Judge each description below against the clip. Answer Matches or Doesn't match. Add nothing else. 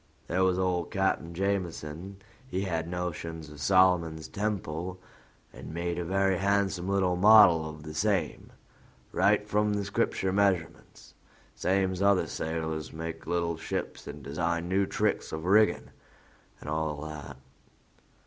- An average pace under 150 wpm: Matches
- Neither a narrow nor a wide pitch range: Matches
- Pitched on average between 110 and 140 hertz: Doesn't match